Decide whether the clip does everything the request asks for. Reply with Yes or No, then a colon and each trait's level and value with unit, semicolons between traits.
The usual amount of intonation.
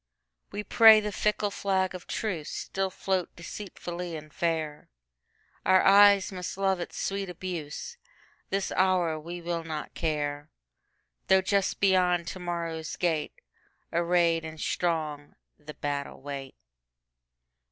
Yes: average, 3.7 semitones